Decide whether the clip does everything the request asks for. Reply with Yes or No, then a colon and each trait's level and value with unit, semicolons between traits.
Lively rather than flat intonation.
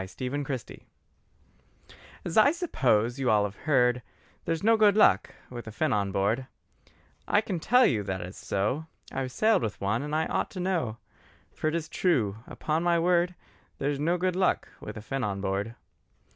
Yes: wide, 8.2 semitones